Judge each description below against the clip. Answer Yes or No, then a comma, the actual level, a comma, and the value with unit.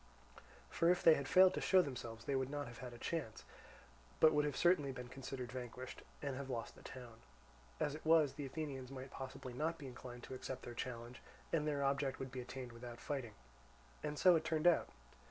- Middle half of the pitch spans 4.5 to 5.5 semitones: No, average, 3.2 semitones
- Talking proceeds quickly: Yes, fast, 210 wpm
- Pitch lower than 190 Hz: Yes, low, 135 Hz